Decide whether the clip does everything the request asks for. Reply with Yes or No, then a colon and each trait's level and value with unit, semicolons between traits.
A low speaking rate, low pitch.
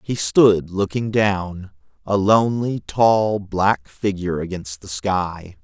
Yes: slow, 130 wpm; very low, 95 Hz